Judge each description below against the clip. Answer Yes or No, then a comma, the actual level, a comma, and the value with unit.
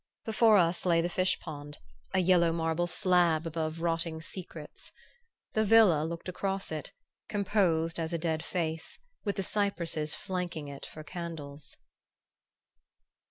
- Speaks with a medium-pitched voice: Yes, medium, 170 Hz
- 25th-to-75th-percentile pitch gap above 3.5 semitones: No, narrow, 2.5 semitones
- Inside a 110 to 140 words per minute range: Yes, slow, 135 wpm